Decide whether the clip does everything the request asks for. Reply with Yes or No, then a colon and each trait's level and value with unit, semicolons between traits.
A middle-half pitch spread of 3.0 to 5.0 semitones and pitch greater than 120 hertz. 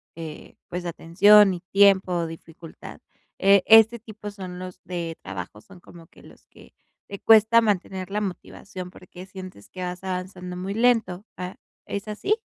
No: narrow, 2.4 semitones; medium, 185 Hz